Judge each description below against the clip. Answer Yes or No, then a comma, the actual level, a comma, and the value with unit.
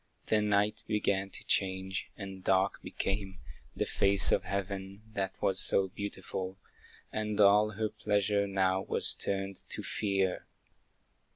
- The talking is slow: Yes, slow, 130 wpm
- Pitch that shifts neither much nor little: No, narrow, 1.2 semitones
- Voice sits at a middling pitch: No, low, 100 Hz